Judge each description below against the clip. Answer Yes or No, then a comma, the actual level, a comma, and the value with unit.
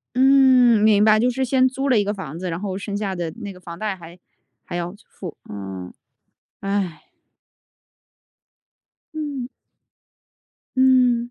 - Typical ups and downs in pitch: No, wide, 5.9 semitones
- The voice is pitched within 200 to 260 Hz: Yes, high, 205 Hz